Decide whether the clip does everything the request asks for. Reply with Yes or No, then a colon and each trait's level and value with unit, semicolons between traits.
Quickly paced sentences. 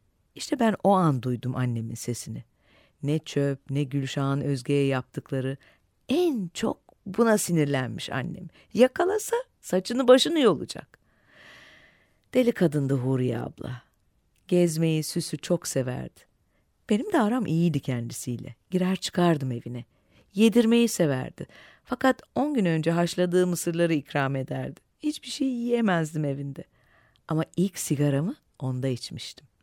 No: average, 115 wpm